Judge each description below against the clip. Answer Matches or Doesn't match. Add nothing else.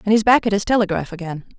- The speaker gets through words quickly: Matches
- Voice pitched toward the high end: Matches